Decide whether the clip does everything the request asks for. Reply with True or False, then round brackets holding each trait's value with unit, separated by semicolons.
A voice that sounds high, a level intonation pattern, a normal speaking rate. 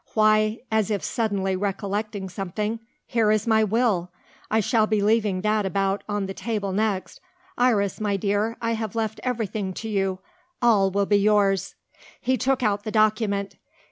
True (210 Hz; 1.9 semitones; 165 wpm)